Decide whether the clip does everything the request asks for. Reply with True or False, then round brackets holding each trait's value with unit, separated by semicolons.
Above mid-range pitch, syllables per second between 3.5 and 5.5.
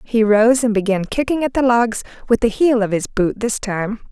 True (225 Hz; 5.0 syllables/s)